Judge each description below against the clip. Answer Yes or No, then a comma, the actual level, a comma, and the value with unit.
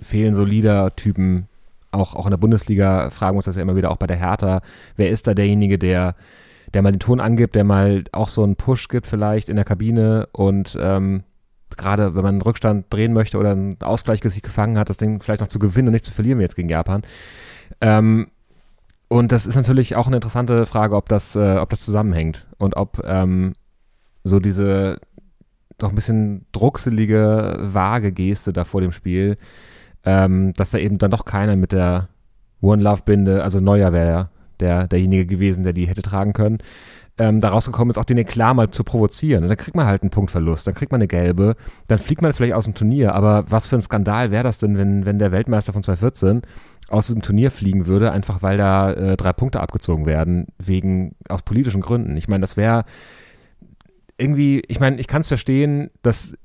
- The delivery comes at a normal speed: No, fast, 205 wpm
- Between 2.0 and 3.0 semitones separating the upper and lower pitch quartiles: Yes, average, 2.7 semitones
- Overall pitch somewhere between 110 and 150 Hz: No, low, 100 Hz